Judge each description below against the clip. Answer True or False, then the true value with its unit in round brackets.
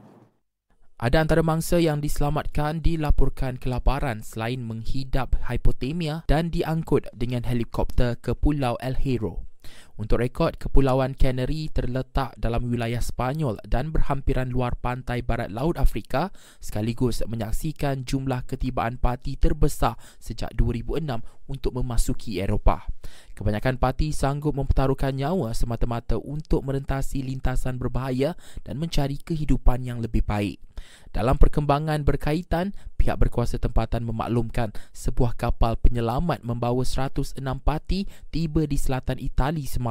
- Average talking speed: True (115 wpm)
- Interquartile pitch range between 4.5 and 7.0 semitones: False (3.3 semitones)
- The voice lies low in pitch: True (130 Hz)